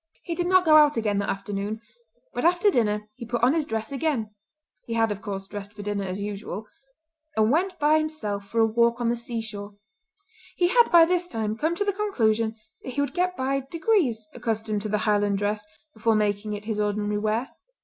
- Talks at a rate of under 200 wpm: No, fast, 205 wpm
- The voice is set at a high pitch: Yes, high, 225 Hz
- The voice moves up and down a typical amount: No, wide, 6.7 semitones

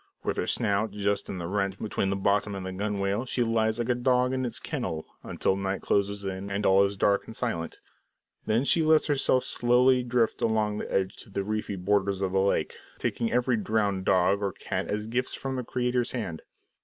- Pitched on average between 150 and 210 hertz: No, low, 105 Hz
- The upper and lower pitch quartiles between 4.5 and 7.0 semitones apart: No, average, 3.7 semitones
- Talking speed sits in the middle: No, fast, 210 wpm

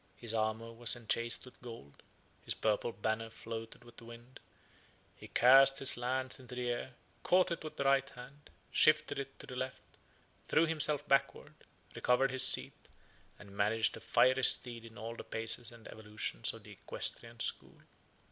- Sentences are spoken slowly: No, average, 170 wpm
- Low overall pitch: Yes, low, 120 Hz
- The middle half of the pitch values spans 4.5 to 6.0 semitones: No, average, 3.0 semitones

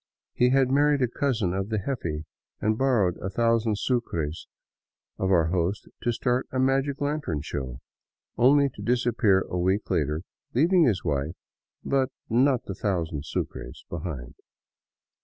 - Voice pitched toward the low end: Yes, low, 110 Hz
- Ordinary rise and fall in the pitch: No, wide, 7.3 semitones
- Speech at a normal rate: Yes, average, 150 wpm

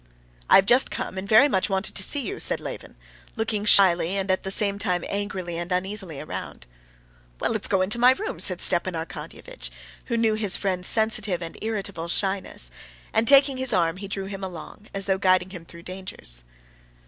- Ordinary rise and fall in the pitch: Yes, average, 3.0 semitones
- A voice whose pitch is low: No, high, 195 Hz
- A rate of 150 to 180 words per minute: No, average, 195 wpm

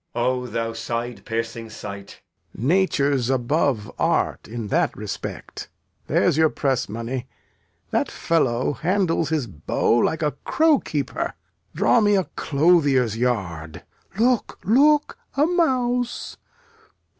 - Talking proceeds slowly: Yes, slow, 125 wpm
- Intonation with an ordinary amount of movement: No, wide, 8.5 semitones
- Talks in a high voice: No, low, 135 Hz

